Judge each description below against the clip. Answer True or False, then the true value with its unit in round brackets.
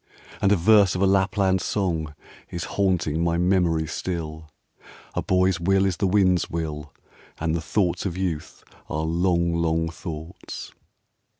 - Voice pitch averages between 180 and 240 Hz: False (85 Hz)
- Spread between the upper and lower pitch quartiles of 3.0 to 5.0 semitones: False (2.6 semitones)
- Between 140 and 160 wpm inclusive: True (145 wpm)